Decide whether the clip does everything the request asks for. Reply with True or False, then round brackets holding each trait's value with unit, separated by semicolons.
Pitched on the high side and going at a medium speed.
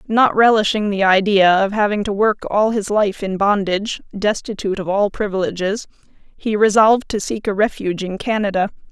True (205 Hz; 170 wpm)